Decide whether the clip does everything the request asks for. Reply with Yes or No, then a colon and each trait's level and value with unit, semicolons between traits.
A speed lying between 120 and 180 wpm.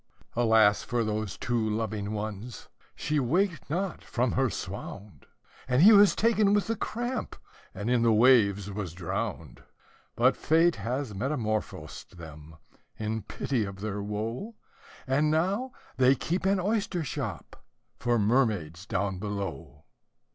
Yes: slow, 135 wpm